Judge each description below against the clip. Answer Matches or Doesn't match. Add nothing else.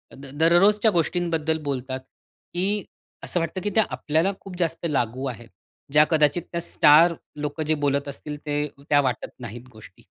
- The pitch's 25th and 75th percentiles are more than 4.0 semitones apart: Doesn't match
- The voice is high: Doesn't match